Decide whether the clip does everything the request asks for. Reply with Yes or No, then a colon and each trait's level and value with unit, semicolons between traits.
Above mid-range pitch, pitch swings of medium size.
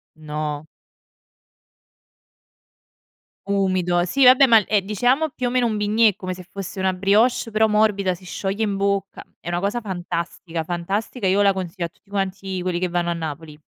Yes: high, 195 Hz; average, 3.3 semitones